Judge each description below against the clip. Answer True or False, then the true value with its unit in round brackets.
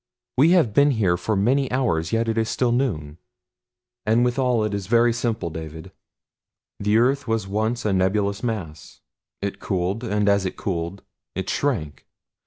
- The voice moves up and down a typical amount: True (4.2 semitones)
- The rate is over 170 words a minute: False (165 wpm)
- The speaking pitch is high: False (110 Hz)